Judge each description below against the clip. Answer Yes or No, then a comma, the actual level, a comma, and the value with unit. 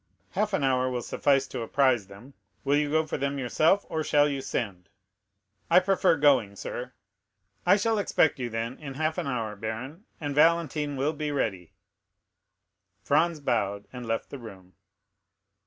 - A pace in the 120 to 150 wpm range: No, average, 165 wpm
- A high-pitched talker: No, medium, 140 Hz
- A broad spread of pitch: No, average, 4.9 semitones